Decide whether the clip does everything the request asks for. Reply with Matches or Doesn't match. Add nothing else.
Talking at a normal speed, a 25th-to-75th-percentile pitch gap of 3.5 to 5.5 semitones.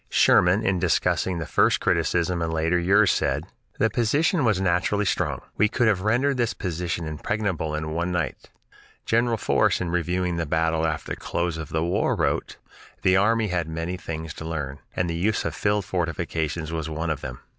Matches